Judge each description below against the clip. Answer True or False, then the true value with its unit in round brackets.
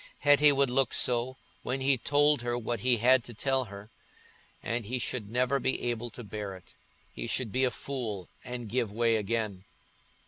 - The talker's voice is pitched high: False (120 Hz)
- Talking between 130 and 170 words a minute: False (180 wpm)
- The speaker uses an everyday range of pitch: True (3.0 semitones)